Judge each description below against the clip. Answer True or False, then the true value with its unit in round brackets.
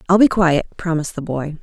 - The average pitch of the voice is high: False (165 Hz)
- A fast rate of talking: True (220 wpm)